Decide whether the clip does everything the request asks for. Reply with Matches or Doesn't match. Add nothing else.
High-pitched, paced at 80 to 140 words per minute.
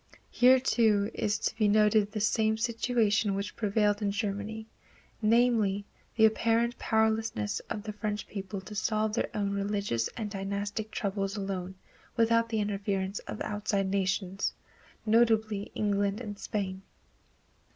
Matches